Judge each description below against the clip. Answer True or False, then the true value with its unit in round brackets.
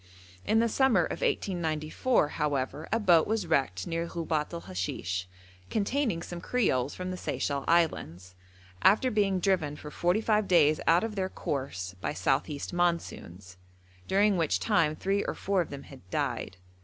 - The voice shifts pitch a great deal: True (5.7 semitones)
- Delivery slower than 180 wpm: True (165 wpm)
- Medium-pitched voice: True (170 Hz)